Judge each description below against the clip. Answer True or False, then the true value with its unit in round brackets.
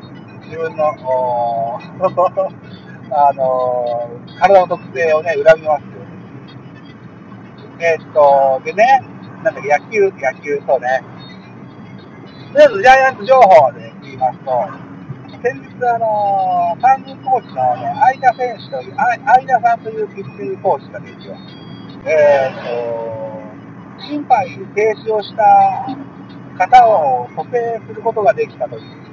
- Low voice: False (190 Hz)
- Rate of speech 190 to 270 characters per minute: True (245 characters per minute)